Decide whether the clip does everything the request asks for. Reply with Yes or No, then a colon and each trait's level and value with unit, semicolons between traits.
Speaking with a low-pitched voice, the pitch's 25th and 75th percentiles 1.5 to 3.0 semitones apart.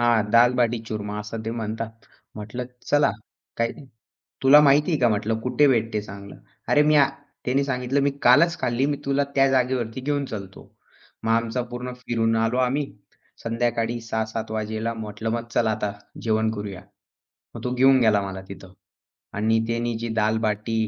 Yes: low, 115 Hz; narrow, 2.6 semitones